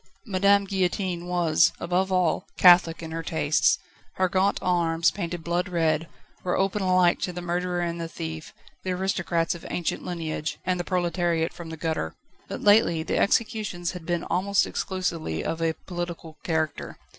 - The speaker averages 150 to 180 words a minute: Yes, average, 165 wpm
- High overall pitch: No, medium, 175 Hz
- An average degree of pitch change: No, narrow, 2.0 semitones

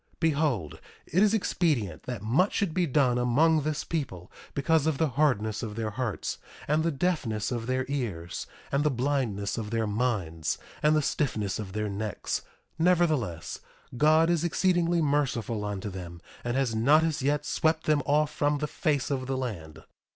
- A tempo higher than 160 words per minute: Yes, average, 175 wpm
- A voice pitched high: No, low, 135 Hz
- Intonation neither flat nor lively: No, wide, 6.2 semitones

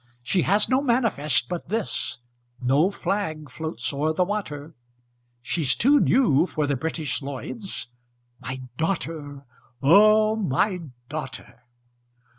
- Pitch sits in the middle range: Yes, medium, 160 Hz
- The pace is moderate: No, slow, 115 wpm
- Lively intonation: Yes, wide, 6.5 semitones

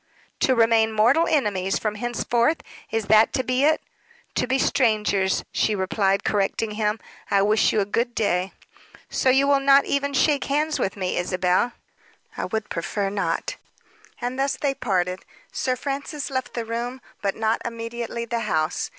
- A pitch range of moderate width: Yes, average, 4.3 semitones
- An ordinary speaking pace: Yes, average, 165 wpm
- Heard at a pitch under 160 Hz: No, high, 230 Hz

